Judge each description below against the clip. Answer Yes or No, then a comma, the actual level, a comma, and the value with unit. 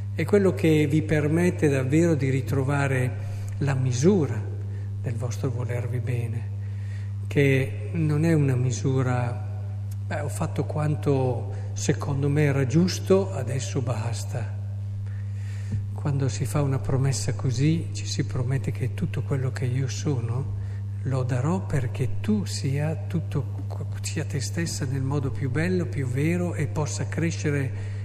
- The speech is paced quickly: No, average, 135 wpm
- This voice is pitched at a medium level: No, low, 115 Hz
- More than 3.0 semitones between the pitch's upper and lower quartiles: Yes, average, 5.2 semitones